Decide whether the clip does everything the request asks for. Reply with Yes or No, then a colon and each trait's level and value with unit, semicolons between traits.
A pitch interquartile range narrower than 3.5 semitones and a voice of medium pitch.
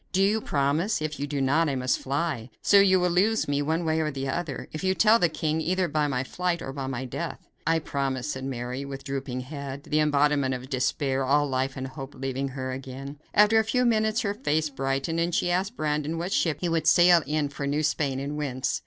No: average, 4.1 semitones; medium, 145 Hz